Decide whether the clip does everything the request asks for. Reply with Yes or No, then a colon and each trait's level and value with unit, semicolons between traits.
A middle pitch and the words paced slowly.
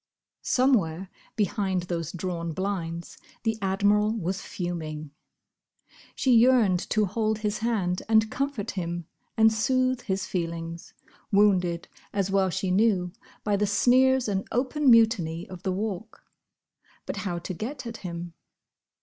No: high, 195 Hz; slow, 130 wpm